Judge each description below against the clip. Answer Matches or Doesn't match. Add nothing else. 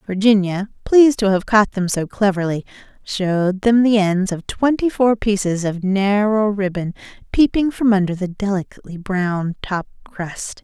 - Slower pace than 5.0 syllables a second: Matches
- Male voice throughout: Doesn't match